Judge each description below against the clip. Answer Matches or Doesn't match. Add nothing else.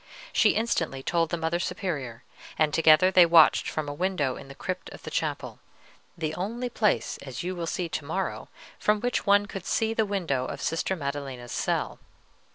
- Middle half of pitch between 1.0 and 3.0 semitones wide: Doesn't match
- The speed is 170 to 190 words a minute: Matches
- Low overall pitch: Doesn't match